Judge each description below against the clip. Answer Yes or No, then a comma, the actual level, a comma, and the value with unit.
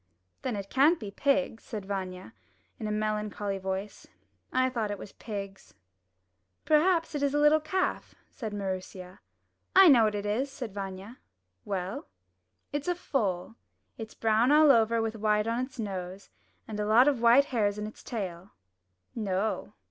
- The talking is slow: No, average, 165 wpm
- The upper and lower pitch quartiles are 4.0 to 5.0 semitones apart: Yes, average, 4.7 semitones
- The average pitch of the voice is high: Yes, high, 215 Hz